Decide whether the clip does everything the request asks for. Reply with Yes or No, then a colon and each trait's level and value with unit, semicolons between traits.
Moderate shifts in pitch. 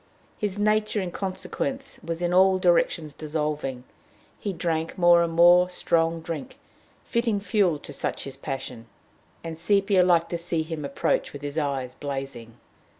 Yes: average, 4.0 semitones